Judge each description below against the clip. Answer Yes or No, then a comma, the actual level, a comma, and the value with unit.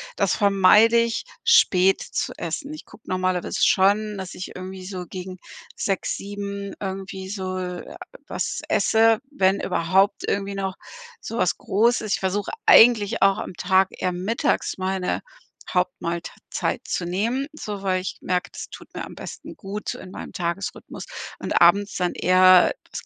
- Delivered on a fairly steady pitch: Yes, narrow, 1.9 semitones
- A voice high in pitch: Yes, high, 195 Hz